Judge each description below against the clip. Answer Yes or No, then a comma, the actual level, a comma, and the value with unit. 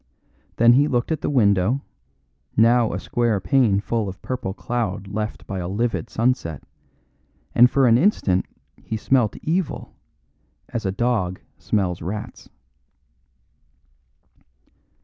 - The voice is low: Yes, low, 115 Hz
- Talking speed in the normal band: No, slow, 120 wpm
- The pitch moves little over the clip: No, average, 4.1 semitones